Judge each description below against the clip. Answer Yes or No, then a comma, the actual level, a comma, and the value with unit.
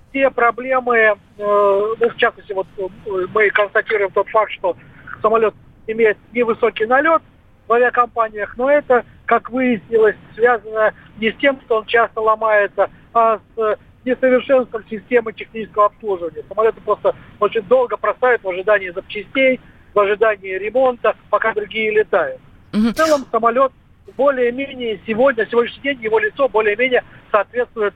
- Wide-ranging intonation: No, average, 2.8 semitones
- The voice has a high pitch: Yes, high, 220 Hz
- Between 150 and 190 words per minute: No, average, 135 wpm